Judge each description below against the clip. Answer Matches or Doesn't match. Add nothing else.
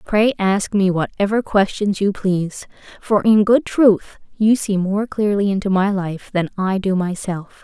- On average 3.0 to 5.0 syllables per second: Matches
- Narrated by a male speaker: Doesn't match